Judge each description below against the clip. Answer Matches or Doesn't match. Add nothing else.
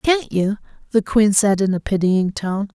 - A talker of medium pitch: Doesn't match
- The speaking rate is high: Doesn't match